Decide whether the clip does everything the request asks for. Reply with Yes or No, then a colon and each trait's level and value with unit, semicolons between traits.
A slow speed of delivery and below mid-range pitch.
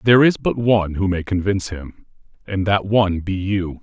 No: fast, 205 wpm; low, 100 Hz